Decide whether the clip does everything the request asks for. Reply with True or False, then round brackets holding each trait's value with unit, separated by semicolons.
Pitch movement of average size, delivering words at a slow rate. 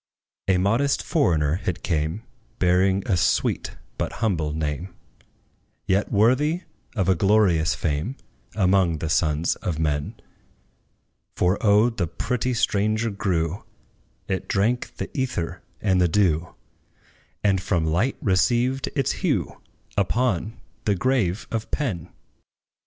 True (4.9 semitones; 120 wpm)